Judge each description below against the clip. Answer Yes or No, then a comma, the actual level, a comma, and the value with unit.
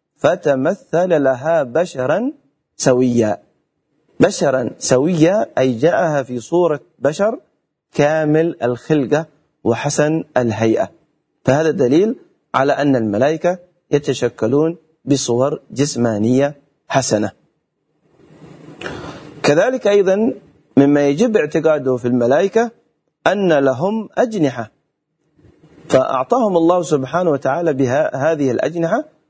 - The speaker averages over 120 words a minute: No, average, 85 wpm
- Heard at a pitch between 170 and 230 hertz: No, medium, 150 Hz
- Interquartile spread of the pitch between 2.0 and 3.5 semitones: No, average, 4.2 semitones